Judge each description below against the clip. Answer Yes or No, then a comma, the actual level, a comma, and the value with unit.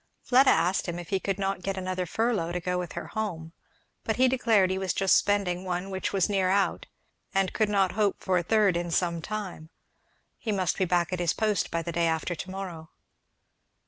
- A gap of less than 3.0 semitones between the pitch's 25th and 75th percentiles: Yes, narrow, 2.4 semitones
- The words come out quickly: Yes, fast, 220 wpm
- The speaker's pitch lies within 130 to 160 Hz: No, medium, 185 Hz